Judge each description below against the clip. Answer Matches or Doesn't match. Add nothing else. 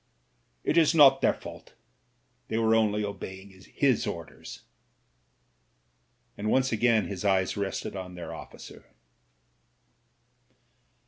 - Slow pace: Matches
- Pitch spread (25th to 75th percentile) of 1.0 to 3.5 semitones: Matches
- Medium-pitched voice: Doesn't match